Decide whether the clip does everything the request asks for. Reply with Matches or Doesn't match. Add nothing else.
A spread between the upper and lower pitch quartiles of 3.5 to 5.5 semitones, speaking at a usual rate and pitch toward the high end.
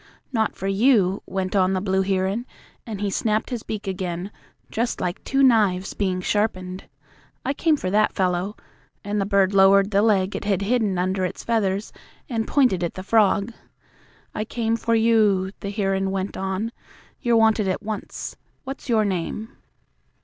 Doesn't match